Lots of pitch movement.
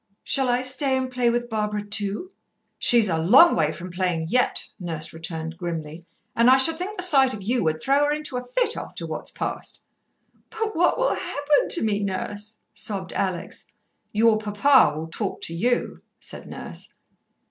Yes: wide, 6.7 semitones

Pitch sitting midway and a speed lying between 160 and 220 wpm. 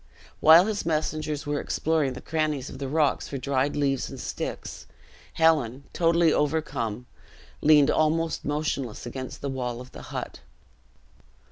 No: medium, 145 Hz; average, 140 wpm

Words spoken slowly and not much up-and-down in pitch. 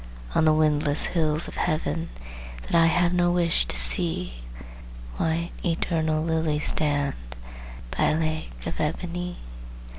Yes: slow, 130 wpm; narrow, 2.2 semitones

